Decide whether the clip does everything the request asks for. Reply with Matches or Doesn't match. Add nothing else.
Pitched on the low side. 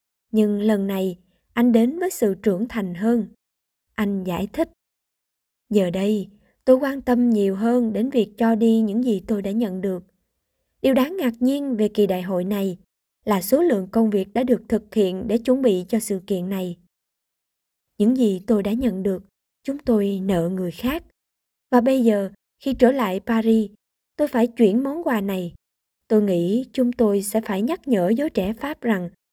Doesn't match